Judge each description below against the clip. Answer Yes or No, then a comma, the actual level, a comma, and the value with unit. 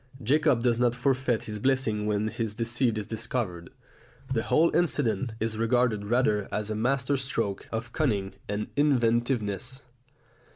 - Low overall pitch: Yes, low, 115 Hz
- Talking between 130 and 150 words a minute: Yes, average, 140 wpm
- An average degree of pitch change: Yes, average, 3.4 semitones